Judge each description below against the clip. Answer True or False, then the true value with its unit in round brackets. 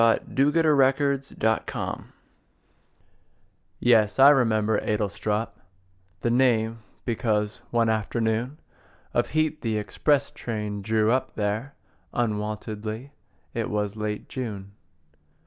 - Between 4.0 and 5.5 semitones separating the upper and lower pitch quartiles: False (3.6 semitones)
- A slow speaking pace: True (95 wpm)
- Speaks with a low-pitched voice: True (110 Hz)